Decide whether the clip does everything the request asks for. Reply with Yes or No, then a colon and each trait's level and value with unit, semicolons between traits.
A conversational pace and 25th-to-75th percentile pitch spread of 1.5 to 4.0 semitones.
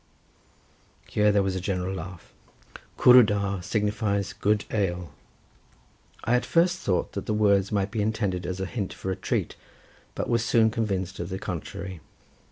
Yes: average, 165 wpm; narrow, 2.4 semitones